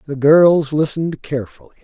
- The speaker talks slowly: Yes, slow, 130 wpm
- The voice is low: No, medium, 150 Hz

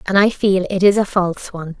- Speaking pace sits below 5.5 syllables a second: No, 6.1 syllables/s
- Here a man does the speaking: No, female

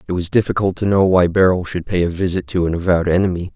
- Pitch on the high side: No, very low, 90 Hz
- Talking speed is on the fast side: Yes, fast, 255 wpm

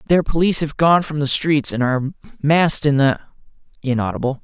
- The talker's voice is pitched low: No, medium, 145 Hz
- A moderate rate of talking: Yes, average, 175 wpm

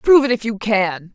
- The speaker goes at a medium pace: No, fast, 265 wpm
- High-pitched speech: Yes, high, 220 Hz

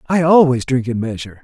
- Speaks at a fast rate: Yes, fast, 210 wpm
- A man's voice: Yes, male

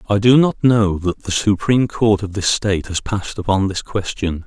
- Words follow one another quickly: Yes, fast, 215 wpm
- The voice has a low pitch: Yes, low, 100 Hz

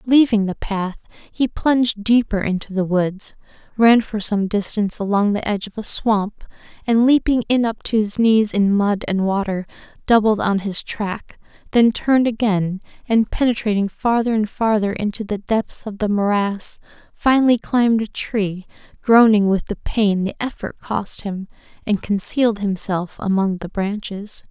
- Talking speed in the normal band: Yes, average, 160 wpm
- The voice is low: No, high, 210 Hz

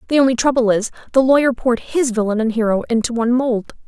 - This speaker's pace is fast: Yes, fast, 215 wpm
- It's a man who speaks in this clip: No, female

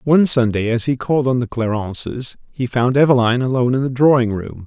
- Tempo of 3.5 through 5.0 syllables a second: No, 6.0 syllables/s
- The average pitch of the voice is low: Yes, low, 125 Hz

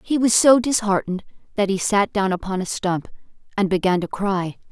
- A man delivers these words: No, female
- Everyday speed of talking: Yes, average, 190 wpm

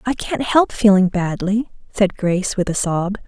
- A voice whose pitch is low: No, high, 200 Hz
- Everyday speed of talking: Yes, average, 185 wpm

